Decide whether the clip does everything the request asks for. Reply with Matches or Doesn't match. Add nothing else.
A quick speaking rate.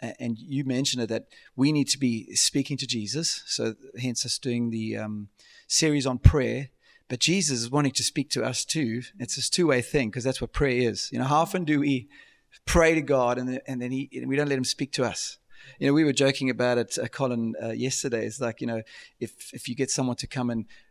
Matches